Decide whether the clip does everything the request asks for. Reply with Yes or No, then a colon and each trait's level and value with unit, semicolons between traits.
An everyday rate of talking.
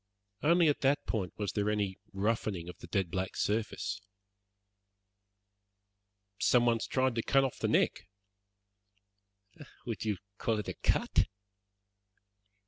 No: slow, 130 wpm